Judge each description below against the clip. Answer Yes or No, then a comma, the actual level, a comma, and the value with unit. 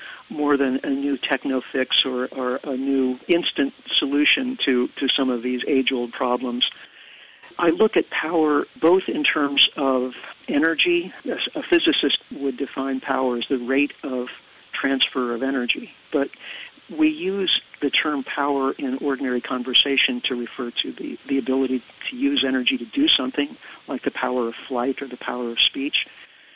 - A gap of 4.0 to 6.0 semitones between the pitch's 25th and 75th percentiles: No, average, 2.7 semitones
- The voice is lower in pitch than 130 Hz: No, low, 135 Hz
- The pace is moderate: Yes, average, 165 wpm